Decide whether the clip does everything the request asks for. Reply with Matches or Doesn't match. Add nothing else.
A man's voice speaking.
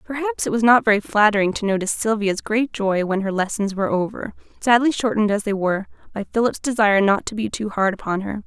Doesn't match